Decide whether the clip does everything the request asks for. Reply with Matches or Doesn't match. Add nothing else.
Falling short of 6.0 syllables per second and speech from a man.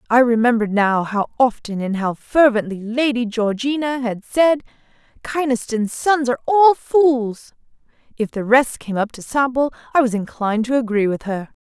Doesn't match